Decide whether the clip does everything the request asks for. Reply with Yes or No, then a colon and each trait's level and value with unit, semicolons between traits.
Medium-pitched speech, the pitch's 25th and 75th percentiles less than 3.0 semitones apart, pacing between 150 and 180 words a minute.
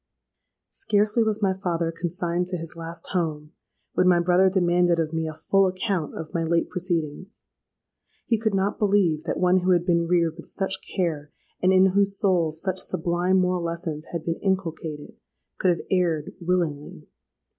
Yes: medium, 175 Hz; narrow, 2.4 semitones; average, 170 wpm